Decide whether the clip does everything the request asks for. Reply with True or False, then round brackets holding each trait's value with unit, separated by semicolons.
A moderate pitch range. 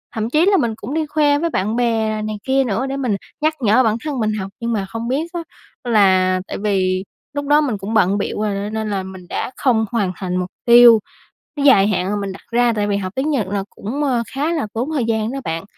True (5.0 semitones)